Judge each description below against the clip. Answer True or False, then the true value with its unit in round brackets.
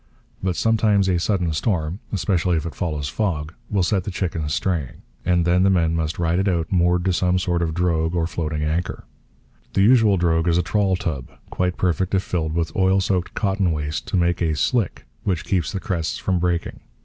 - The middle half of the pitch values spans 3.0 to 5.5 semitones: False (2.5 semitones)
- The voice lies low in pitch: True (90 Hz)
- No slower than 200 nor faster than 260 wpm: True (205 wpm)